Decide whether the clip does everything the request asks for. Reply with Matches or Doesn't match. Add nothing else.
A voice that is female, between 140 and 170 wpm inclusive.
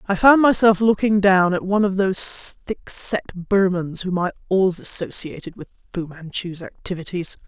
Matches